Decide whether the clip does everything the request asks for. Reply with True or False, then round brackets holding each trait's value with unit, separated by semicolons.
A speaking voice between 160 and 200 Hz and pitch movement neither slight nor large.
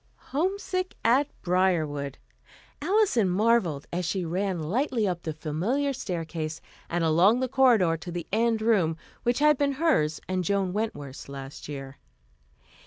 False (185 Hz; 7.4 semitones)